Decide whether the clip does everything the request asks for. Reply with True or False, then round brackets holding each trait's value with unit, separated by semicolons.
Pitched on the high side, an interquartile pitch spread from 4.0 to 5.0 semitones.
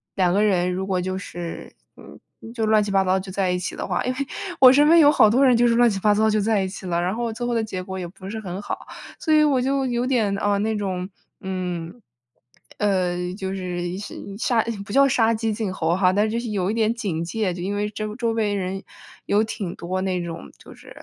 False (205 Hz; 3.6 semitones)